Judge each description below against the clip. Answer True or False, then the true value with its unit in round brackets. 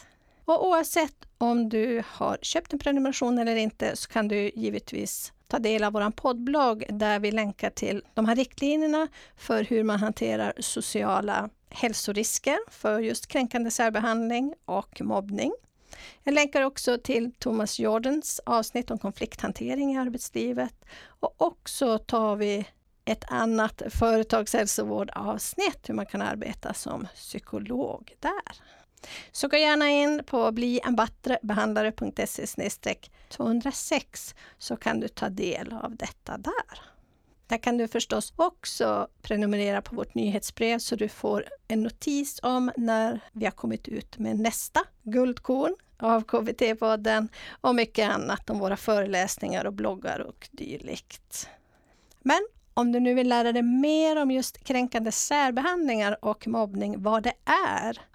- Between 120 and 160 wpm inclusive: True (135 wpm)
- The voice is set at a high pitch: True (235 Hz)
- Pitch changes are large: False (3.4 semitones)